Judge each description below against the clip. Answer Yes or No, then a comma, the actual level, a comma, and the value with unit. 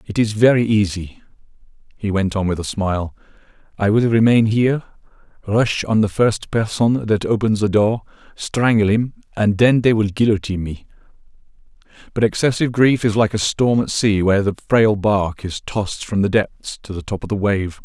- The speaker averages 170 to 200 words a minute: Yes, average, 185 wpm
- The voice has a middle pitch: No, low, 105 Hz